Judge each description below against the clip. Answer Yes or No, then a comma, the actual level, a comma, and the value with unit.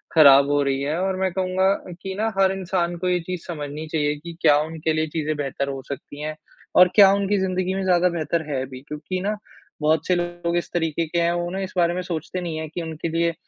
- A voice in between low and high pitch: Yes, medium, 170 Hz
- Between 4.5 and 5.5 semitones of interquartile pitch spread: No, average, 3.2 semitones